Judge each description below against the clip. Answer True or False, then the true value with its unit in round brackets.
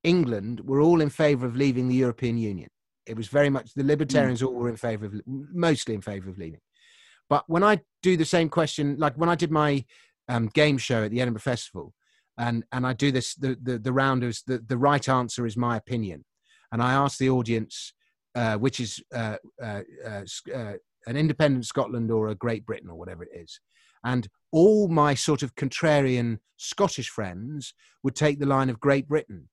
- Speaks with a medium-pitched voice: False (130 Hz)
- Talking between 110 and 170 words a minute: False (200 wpm)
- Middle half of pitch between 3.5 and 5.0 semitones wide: True (3.9 semitones)